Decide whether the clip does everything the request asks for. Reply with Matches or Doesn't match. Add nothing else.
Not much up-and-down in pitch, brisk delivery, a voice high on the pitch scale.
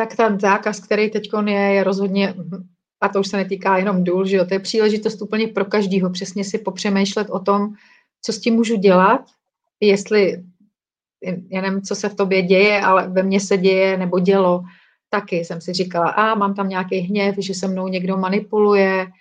Matches